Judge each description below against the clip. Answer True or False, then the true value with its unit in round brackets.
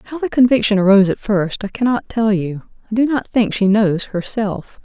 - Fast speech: True (210 wpm)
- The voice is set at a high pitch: True (215 Hz)